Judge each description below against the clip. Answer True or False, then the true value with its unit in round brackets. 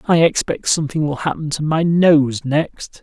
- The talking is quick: False (180 wpm)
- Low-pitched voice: False (155 Hz)